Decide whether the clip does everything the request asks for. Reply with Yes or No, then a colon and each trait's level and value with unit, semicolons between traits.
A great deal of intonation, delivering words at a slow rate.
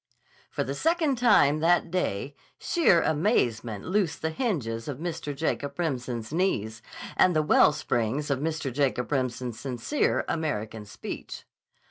Yes: wide, 5.7 semitones; slow, 130 wpm